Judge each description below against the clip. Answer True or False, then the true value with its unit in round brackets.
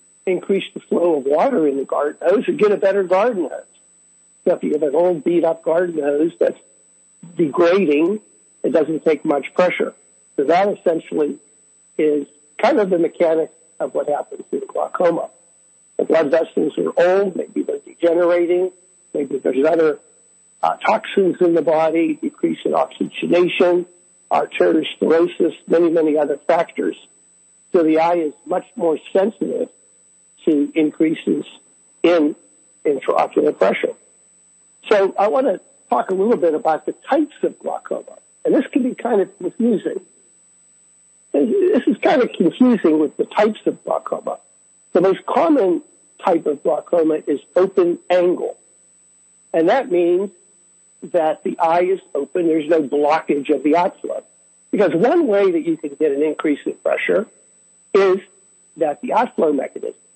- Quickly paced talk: False (150 wpm)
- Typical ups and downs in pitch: False (6.6 semitones)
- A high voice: False (180 Hz)